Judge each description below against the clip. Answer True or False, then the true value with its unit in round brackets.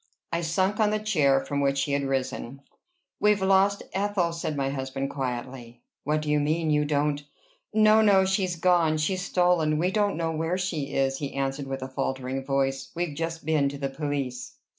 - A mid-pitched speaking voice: True (150 Hz)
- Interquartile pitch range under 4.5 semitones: False (4.8 semitones)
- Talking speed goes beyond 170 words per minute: True (185 wpm)